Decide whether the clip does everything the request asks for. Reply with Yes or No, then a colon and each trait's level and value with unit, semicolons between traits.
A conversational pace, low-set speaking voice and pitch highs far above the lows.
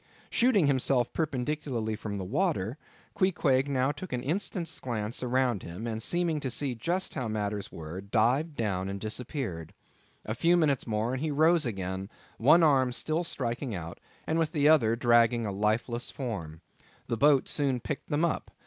Yes: average, 170 wpm; low, 125 Hz; wide, 5.7 semitones